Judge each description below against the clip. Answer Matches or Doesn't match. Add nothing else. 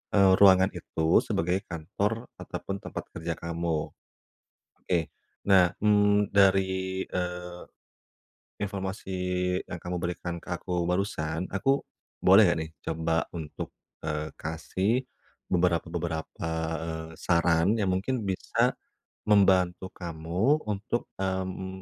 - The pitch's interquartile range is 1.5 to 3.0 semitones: Matches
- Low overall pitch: Matches